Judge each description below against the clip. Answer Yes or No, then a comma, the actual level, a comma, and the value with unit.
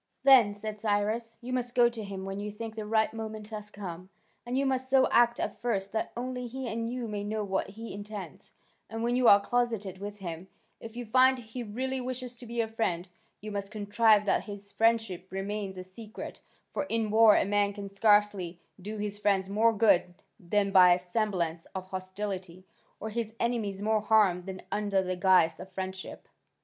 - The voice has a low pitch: No, high, 210 Hz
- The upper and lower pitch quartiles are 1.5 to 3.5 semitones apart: Yes, average, 2.9 semitones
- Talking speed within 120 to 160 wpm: No, average, 200 wpm